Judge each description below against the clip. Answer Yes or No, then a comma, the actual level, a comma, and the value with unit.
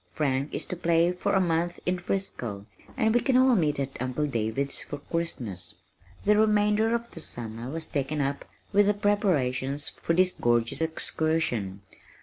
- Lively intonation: Yes, wide, 6.9 semitones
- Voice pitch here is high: No, medium, 160 Hz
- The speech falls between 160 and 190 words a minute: Yes, average, 165 wpm